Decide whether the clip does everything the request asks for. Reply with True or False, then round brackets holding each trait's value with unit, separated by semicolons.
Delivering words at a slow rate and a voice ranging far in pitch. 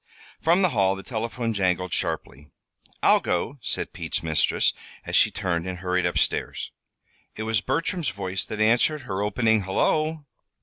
False (160 wpm; 5.7 semitones)